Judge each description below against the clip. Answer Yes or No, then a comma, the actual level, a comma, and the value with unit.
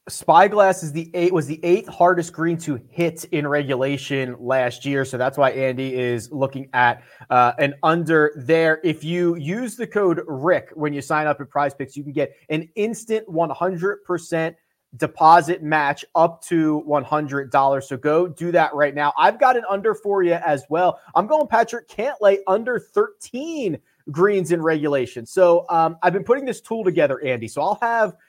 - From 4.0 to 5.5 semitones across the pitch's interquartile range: Yes, average, 4.8 semitones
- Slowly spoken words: No, average, 190 wpm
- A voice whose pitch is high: No, medium, 165 Hz